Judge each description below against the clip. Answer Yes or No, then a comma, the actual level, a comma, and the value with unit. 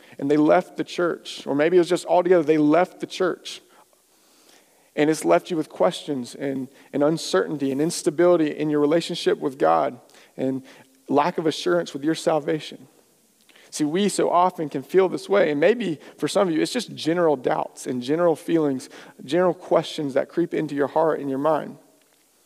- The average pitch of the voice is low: No, medium, 155 Hz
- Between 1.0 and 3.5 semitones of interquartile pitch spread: Yes, average, 3.1 semitones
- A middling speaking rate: Yes, average, 185 wpm